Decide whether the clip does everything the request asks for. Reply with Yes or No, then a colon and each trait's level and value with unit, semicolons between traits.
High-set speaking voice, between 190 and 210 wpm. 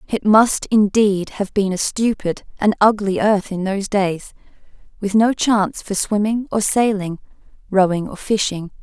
No: high, 200 Hz; average, 155 wpm